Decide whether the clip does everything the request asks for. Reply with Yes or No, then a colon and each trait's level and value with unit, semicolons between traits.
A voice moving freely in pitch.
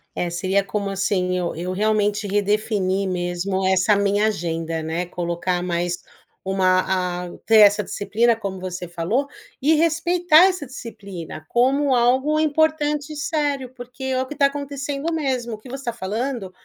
Yes: wide, 6.9 semitones